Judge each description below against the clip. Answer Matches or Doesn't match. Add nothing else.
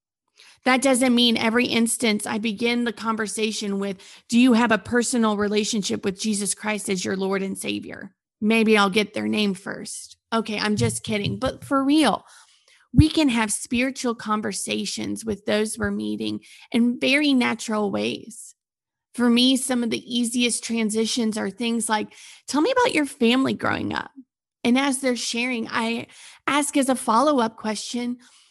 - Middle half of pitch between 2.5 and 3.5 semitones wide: Matches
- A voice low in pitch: Doesn't match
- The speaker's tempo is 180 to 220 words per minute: Doesn't match